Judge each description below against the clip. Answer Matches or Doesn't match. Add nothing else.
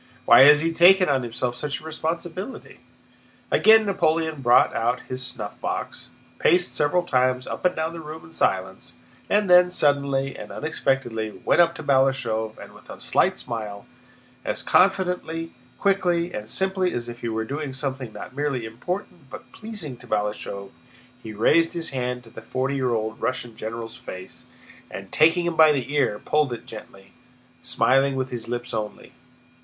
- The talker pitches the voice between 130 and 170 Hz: Matches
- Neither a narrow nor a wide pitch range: Doesn't match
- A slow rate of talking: Doesn't match